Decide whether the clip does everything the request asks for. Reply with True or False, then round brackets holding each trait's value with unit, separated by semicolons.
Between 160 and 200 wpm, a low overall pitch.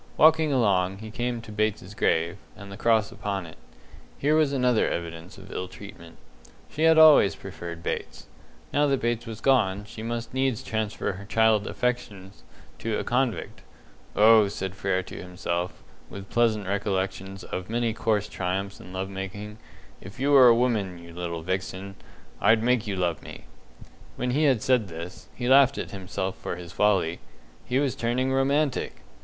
True (170 wpm; 105 Hz)